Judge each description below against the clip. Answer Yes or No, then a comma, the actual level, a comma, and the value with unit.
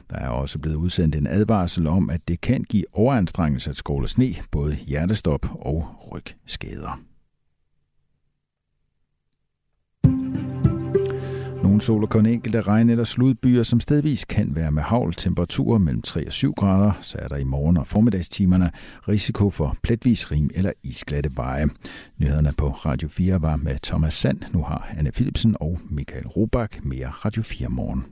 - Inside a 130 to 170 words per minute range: Yes, average, 155 wpm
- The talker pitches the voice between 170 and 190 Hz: No, very low, 90 Hz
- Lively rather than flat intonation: Yes, wide, 6.7 semitones